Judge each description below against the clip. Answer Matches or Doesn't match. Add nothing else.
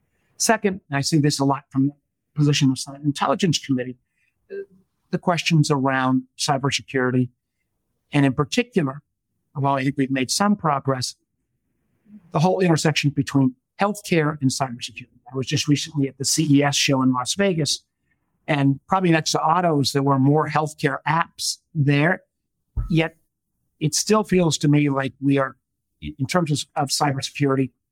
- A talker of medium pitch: Matches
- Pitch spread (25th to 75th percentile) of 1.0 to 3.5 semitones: Matches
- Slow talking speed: Doesn't match